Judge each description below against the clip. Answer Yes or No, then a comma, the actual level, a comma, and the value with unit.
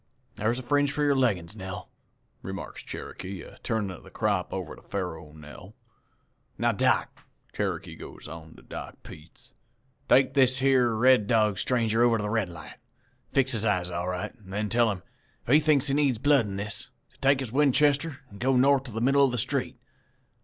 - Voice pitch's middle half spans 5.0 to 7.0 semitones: Yes, average, 5.3 semitones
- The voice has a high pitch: No, low, 115 Hz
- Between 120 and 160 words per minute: No, average, 195 wpm